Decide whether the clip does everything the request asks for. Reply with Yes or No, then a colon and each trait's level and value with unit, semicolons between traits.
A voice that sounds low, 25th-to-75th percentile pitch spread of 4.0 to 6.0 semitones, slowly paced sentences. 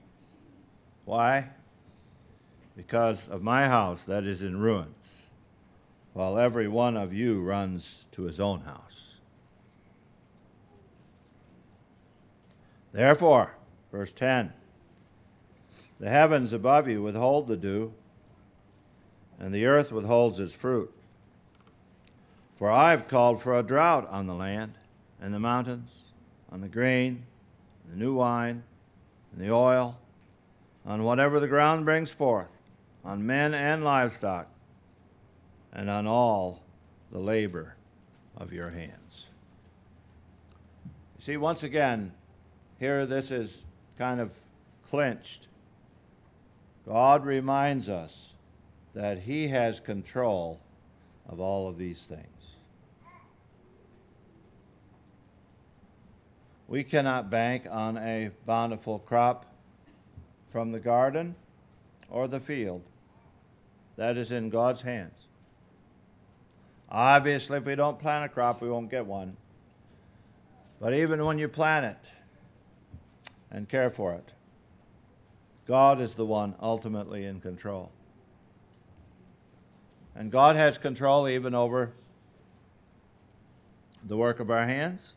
Yes: low, 110 Hz; average, 4.3 semitones; slow, 110 wpm